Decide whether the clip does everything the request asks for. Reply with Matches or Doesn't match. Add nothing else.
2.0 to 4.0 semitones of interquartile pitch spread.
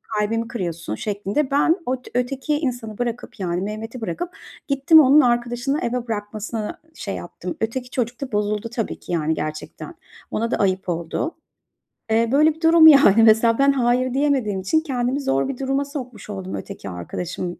Doesn't match